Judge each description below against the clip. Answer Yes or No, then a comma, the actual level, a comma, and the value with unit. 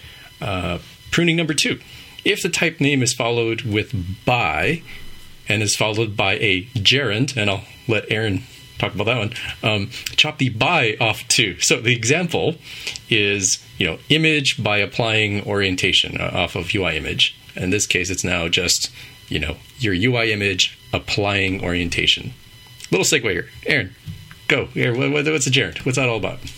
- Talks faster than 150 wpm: Yes, average, 165 wpm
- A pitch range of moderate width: Yes, average, 4.4 semitones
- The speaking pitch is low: Yes, low, 115 Hz